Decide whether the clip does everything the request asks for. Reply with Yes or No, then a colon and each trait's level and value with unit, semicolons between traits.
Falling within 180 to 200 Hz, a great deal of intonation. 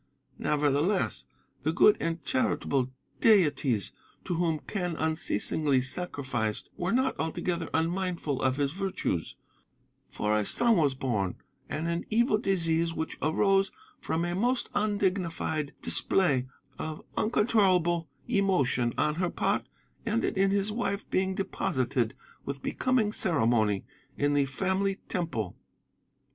No: medium, 165 Hz; wide, 5.8 semitones